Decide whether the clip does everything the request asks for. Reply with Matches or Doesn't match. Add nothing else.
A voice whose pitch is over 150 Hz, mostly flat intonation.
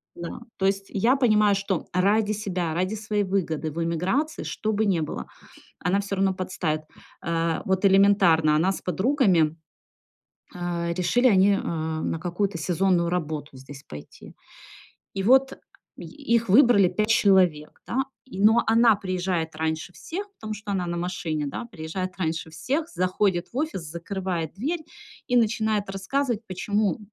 Doesn't match